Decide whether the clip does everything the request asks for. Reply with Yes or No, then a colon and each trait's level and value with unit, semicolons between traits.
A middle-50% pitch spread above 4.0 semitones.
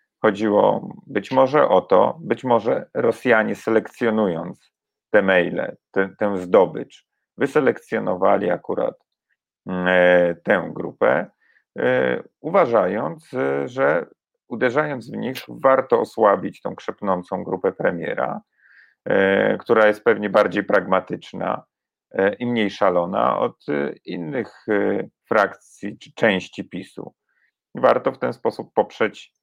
No: average, 2.8 semitones